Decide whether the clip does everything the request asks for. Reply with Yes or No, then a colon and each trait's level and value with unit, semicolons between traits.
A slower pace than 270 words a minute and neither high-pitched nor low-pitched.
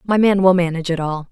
No: fast, 275 wpm; medium, 180 Hz